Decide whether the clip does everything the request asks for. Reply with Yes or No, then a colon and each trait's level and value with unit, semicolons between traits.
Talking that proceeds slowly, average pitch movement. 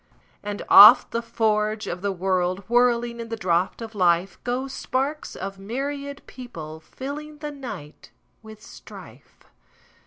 Yes: slow, 120 wpm; average, 5.0 semitones